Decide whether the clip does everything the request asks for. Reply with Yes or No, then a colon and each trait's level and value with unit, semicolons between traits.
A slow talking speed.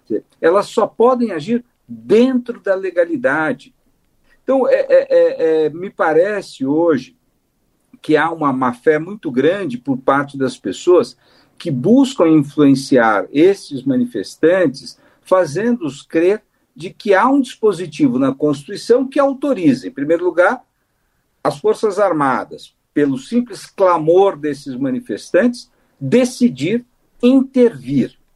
Yes: slow, 110 wpm